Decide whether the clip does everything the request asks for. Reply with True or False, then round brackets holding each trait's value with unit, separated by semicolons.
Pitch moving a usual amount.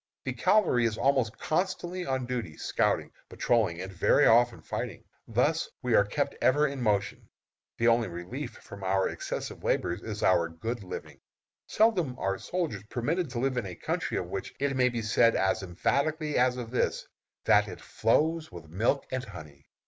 False (5.9 semitones)